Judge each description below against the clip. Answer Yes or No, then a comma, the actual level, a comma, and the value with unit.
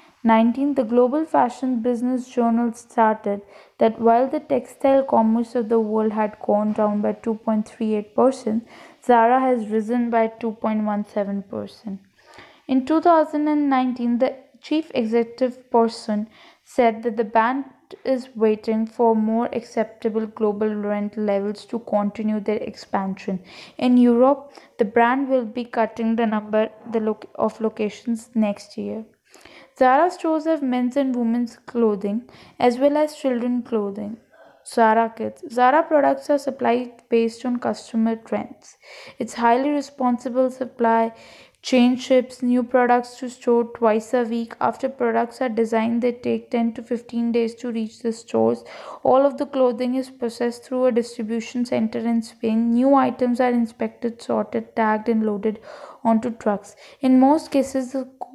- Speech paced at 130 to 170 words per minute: Yes, average, 140 wpm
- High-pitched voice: Yes, high, 235 Hz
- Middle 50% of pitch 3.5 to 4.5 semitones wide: No, narrow, 2.4 semitones